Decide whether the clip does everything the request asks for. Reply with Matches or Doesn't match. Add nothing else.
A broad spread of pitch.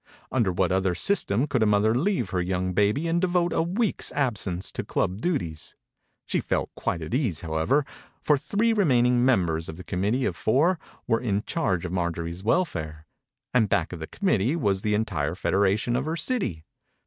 Matches